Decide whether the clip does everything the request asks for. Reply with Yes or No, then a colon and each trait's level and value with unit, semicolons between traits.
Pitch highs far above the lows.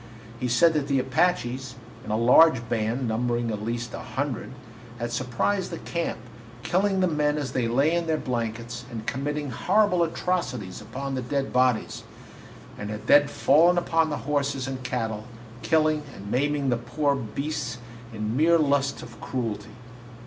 No: average, 4.3 semitones